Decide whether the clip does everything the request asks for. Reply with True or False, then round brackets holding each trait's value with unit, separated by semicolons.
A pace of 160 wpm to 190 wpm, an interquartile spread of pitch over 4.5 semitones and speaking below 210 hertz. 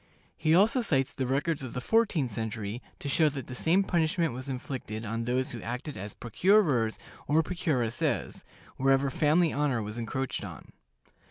True (165 wpm; 5.1 semitones; 135 Hz)